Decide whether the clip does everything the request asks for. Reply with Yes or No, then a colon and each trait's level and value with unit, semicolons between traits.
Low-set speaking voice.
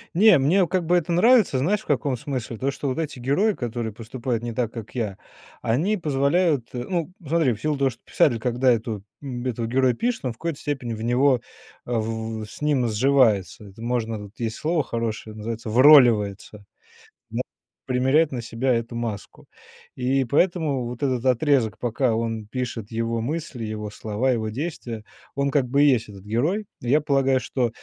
Yes: low, 125 Hz